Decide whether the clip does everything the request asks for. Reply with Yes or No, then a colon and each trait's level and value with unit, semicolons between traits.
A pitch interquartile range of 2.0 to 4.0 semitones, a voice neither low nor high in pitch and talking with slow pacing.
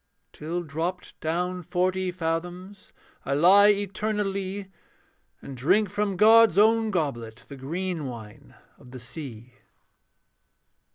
No: average, 5.3 semitones; medium, 180 Hz; slow, 110 wpm